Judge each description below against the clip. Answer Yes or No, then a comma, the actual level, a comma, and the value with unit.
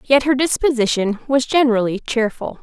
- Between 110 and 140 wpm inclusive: Yes, slow, 135 wpm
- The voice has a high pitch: Yes, very high, 250 Hz